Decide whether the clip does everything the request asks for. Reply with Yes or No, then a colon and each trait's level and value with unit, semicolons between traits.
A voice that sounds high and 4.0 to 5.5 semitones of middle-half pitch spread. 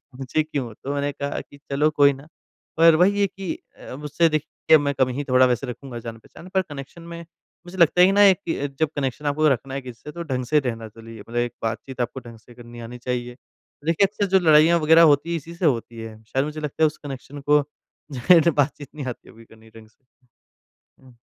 No: medium, 140 Hz; average, 4.4 semitones